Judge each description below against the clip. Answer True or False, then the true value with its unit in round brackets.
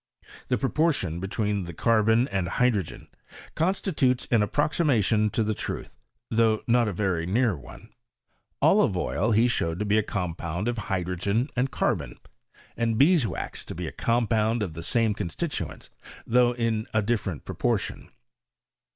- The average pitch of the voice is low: True (110 Hz)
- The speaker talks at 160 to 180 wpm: False (150 wpm)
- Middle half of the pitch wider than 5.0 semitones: False (4.1 semitones)